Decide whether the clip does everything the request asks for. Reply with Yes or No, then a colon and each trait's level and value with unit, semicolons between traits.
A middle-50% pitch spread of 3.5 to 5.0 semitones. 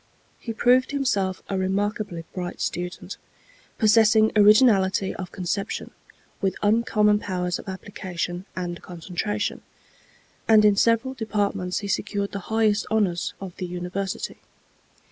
No: average, 2.7 semitones